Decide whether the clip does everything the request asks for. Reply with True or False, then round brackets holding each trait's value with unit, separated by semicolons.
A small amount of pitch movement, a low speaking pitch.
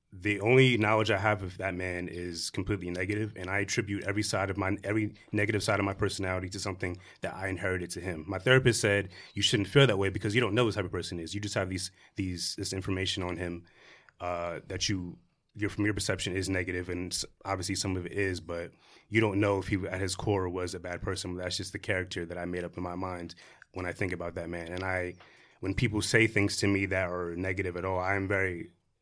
True (2.2 semitones; 95 Hz)